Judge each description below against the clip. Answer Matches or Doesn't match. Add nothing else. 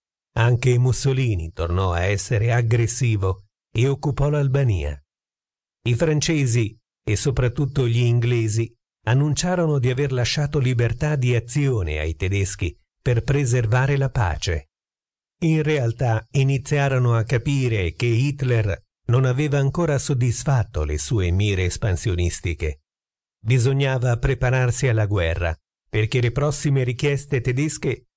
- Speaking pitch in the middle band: Doesn't match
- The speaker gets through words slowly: Matches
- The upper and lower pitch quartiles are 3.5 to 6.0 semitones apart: Matches